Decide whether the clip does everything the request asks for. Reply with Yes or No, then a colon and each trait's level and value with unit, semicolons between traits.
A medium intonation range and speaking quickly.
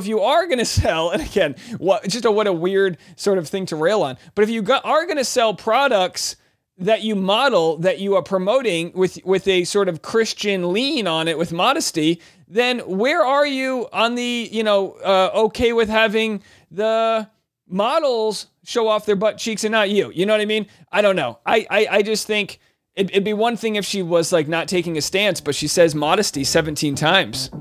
Yes: average, 4.1 semitones; fast, 220 wpm